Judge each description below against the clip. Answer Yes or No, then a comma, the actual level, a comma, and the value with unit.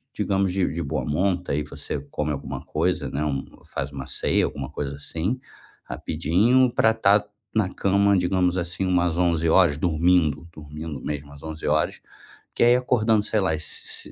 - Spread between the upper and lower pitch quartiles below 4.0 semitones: No, average, 4.5 semitones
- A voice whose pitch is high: No, very low, 85 Hz